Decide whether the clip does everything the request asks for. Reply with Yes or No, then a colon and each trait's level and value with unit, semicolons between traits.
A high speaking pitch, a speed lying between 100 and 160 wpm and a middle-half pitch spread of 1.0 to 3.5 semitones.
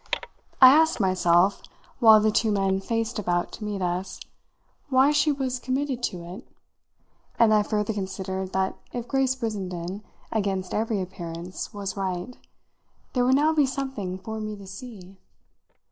No: high, 210 Hz; average, 150 wpm; average, 4.8 semitones